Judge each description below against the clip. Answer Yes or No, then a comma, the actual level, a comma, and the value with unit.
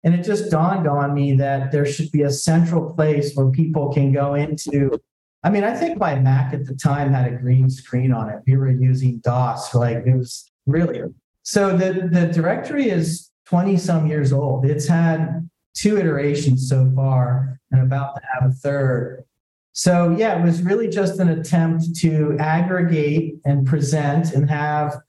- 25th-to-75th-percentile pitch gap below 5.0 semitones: Yes, average, 3.9 semitones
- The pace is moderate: Yes, average, 180 wpm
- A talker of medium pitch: Yes, medium, 150 Hz